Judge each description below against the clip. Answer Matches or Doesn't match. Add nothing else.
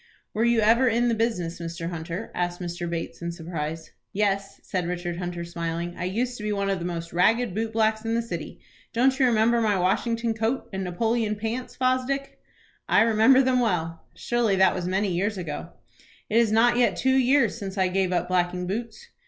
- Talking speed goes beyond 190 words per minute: Matches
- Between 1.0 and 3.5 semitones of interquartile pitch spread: Doesn't match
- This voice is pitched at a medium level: Doesn't match